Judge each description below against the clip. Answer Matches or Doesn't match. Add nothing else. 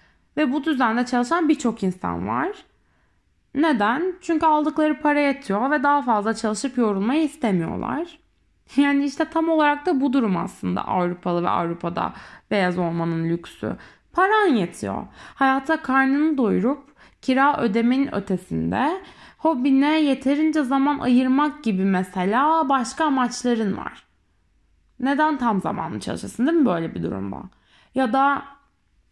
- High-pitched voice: Matches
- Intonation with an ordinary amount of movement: Doesn't match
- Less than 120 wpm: Doesn't match